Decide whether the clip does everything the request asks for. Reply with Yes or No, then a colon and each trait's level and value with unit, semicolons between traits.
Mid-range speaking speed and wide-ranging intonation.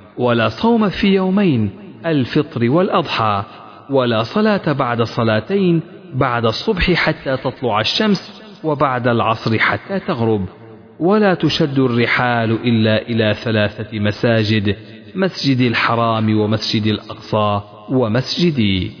Yes: average, 100 wpm; wide, 6.9 semitones